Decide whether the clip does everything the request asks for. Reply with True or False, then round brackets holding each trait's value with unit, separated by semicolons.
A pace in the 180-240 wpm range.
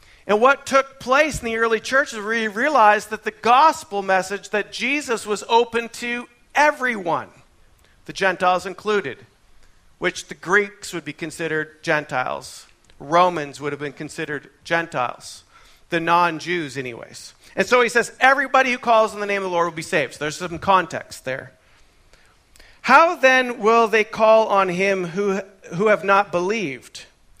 False (160 wpm)